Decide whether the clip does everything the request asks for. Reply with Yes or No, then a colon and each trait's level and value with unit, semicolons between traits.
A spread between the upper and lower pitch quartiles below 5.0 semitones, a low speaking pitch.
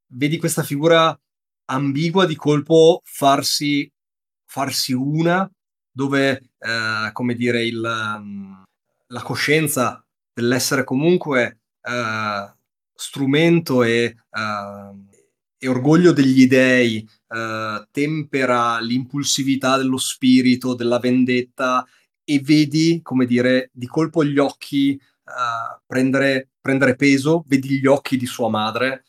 Yes: average, 2.8 semitones; low, 130 Hz